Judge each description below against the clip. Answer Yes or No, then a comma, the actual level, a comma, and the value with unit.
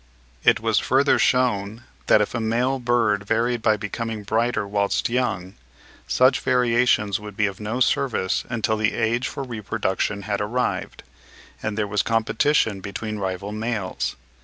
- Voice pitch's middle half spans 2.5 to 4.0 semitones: Yes, average, 2.9 semitones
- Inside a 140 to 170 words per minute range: Yes, average, 150 wpm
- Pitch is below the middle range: Yes, low, 110 Hz